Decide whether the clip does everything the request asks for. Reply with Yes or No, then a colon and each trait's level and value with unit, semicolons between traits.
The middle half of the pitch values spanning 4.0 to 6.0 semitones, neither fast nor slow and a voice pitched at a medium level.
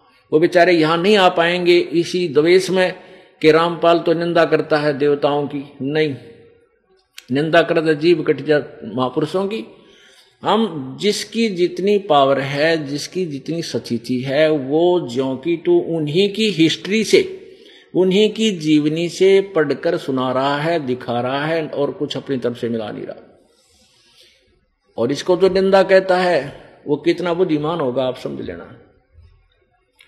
Yes: average, 4.3 semitones; average, 145 wpm; medium, 165 Hz